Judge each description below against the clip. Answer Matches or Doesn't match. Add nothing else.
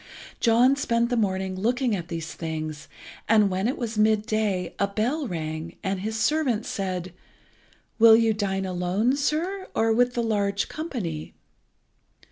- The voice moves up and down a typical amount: Matches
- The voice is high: Matches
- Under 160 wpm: Matches